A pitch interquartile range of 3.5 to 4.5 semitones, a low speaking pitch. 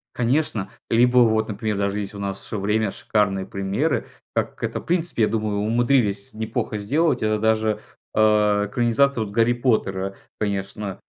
No: average, 2.8 semitones; low, 110 Hz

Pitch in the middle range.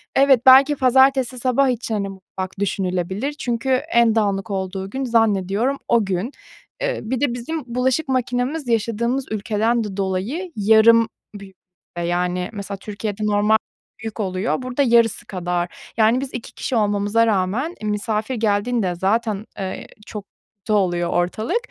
No: high, 220 Hz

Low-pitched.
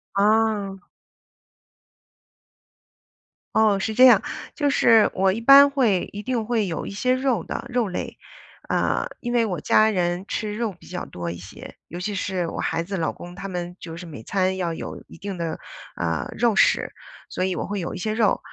No: high, 200 Hz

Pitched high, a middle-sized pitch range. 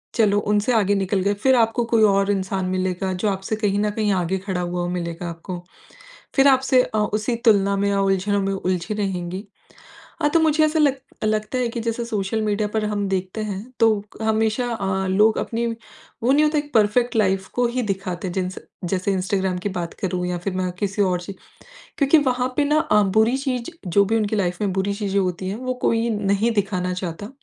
Yes: high, 205 Hz; average, 3.2 semitones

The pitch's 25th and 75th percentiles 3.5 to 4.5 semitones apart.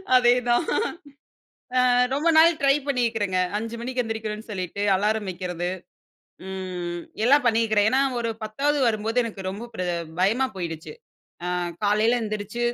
Yes: average, 3.8 semitones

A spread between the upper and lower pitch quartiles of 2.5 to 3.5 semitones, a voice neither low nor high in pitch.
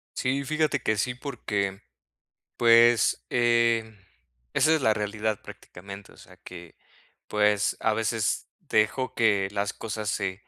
No: average, 2.8 semitones; low, 110 Hz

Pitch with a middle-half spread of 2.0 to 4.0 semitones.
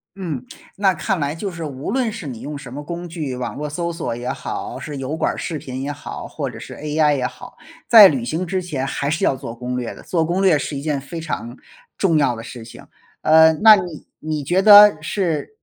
No: average, 4.4 semitones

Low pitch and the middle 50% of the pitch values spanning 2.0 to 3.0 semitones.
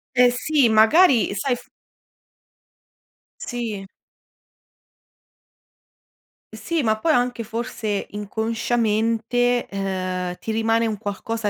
No: high, 225 Hz; average, 2.7 semitones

